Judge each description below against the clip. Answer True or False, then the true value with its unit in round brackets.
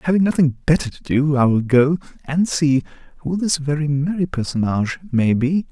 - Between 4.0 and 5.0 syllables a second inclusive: False (5.2 syllables/s)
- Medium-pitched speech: True (145 Hz)